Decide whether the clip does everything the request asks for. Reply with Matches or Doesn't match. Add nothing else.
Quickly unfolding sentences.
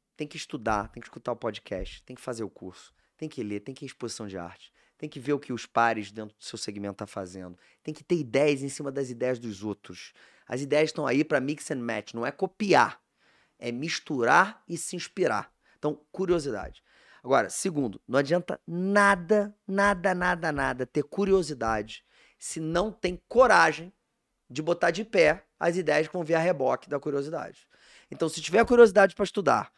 Matches